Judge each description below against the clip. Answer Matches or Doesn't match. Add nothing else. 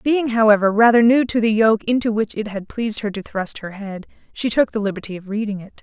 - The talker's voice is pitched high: Matches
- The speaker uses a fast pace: Matches